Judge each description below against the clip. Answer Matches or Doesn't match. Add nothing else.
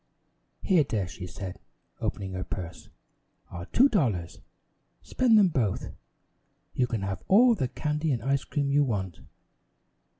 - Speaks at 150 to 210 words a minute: Doesn't match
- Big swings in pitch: Matches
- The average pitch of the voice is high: Doesn't match